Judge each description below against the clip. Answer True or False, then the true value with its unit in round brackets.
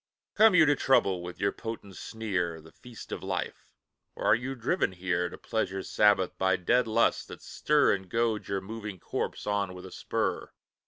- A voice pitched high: False (100 Hz)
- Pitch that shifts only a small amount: False (3.8 semitones)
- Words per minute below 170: False (190 wpm)